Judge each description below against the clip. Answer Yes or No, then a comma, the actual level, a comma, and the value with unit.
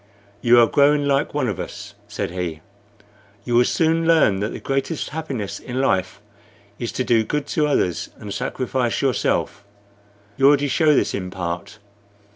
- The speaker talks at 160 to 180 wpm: Yes, average, 165 wpm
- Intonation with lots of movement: Yes, wide, 6.2 semitones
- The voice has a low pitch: Yes, low, 130 Hz